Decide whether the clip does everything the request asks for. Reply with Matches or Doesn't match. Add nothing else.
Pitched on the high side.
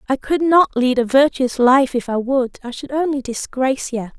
Matches